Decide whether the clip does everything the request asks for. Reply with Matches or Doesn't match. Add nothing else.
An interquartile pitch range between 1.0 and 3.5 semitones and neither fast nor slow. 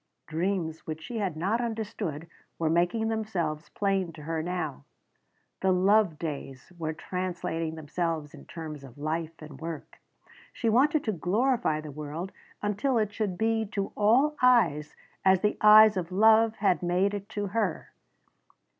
Doesn't match